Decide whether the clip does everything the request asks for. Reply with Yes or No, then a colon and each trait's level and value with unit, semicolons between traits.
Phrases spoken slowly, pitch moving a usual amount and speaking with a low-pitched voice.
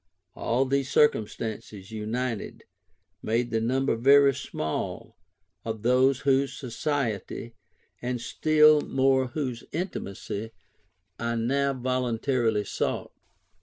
Yes: slow, 95 wpm; average, 3.2 semitones; low, 125 Hz